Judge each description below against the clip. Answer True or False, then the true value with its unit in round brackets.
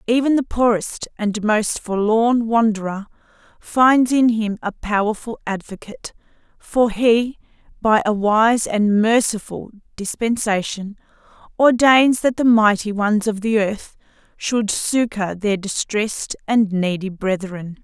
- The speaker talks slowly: True (120 wpm)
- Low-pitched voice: False (215 Hz)